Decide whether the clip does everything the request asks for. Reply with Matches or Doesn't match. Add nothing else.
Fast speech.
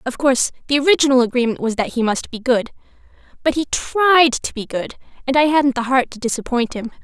Matches